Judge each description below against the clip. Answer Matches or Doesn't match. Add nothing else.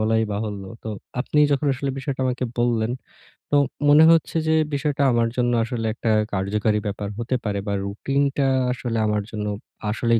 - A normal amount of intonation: Matches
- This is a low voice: Matches